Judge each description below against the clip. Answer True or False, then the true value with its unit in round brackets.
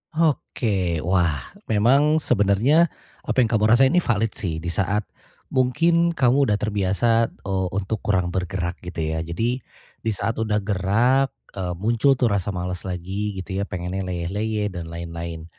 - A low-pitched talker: True (100 Hz)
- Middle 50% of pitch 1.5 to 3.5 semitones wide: False (4.6 semitones)